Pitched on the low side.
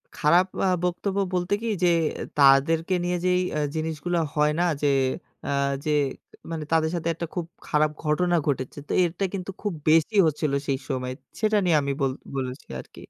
No: medium, 160 Hz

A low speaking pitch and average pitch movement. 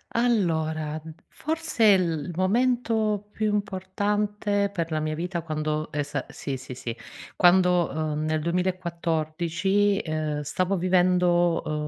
No: medium, 175 Hz; average, 4.4 semitones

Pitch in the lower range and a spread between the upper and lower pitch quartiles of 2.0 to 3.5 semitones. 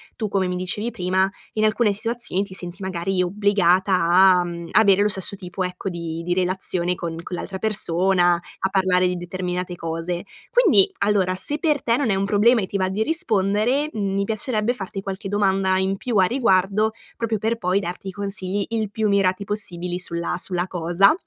No: high, 190 Hz; narrow, 2.5 semitones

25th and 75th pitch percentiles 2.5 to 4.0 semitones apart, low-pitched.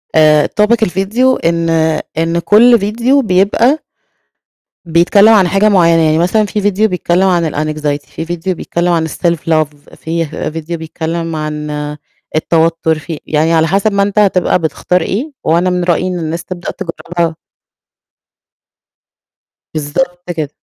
No: average, 3.3 semitones; medium, 170 Hz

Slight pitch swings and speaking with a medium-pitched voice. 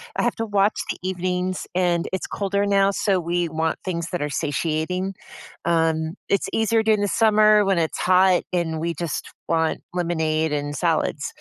No: average, 3.4 semitones; medium, 175 Hz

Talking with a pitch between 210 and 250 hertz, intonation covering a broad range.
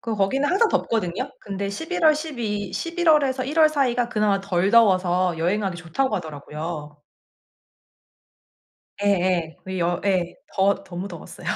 No: high, 200 Hz; wide, 6.6 semitones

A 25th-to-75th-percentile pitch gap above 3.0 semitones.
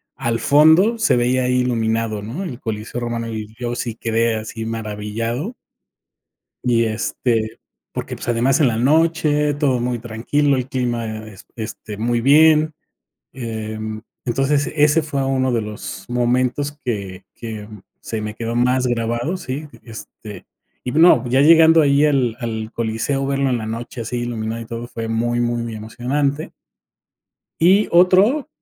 Yes: average, 3.8 semitones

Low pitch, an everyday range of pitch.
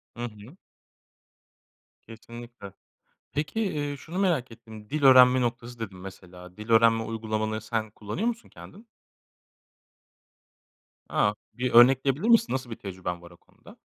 Yes: low, 115 Hz; average, 4.1 semitones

